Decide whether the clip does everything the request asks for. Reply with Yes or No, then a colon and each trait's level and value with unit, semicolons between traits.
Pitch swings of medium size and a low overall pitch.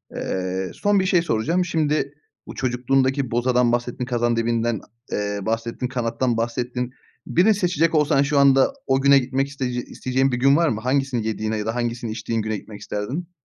Yes: average, 3.3 semitones; low, 125 Hz